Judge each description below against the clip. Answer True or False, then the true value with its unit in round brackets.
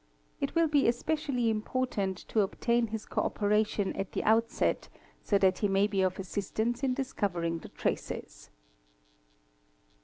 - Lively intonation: False (3.9 semitones)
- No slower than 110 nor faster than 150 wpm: True (145 wpm)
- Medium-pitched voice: False (215 Hz)